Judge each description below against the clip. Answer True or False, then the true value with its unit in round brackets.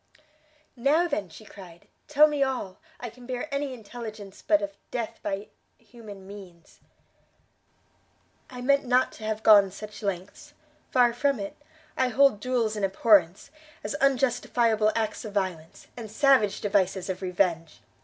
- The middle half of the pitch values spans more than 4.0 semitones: True (4.4 semitones)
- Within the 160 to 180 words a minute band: False (145 wpm)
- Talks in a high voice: True (220 Hz)